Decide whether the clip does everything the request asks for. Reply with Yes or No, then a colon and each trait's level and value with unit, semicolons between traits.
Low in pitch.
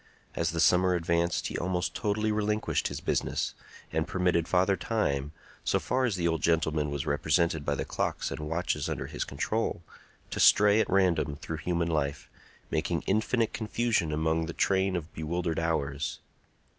Yes: very low, 85 Hz